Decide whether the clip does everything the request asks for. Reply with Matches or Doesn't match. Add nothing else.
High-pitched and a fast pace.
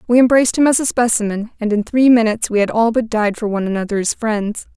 Matches